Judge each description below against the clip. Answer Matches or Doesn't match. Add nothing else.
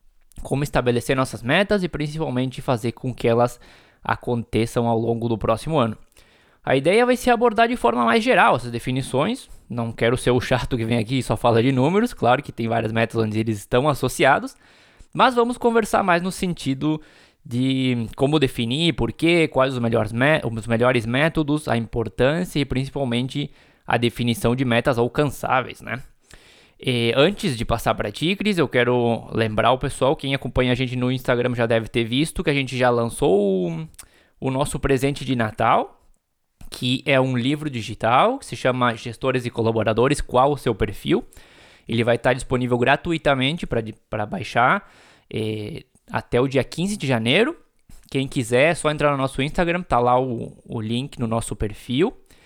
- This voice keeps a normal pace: Matches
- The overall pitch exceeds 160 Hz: Doesn't match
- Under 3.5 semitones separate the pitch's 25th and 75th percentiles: Doesn't match